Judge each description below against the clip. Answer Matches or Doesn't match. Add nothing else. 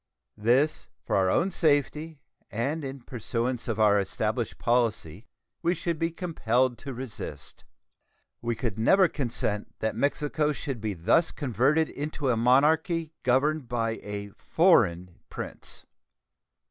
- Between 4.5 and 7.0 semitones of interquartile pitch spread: Matches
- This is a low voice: Matches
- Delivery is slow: Matches